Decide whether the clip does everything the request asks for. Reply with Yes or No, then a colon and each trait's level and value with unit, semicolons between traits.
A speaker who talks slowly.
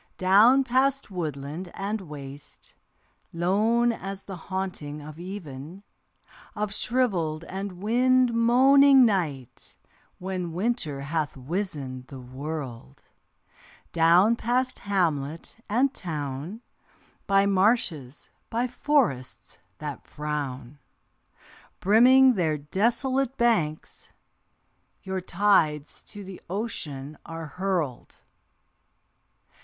Yes: slow, 90 wpm